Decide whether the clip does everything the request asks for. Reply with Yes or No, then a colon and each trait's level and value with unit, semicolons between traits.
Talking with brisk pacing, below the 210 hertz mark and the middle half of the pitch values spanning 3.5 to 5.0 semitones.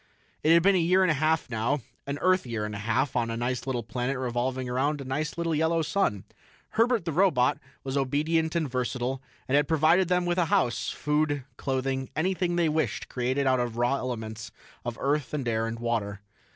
Yes: fast, 210 wpm; low, 135 Hz; average, 4.7 semitones